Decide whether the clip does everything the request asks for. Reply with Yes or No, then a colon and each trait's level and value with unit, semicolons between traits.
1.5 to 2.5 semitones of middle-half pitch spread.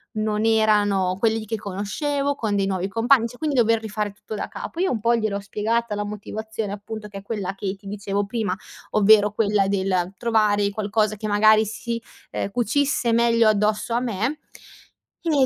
Yes: narrow, 2.2 semitones